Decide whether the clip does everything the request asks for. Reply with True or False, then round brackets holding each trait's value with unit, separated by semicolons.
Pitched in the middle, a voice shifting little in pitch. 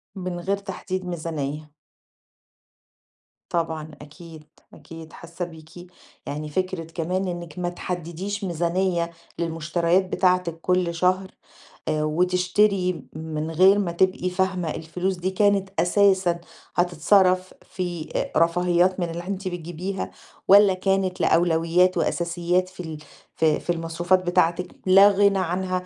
True (175 Hz; 2.0 semitones)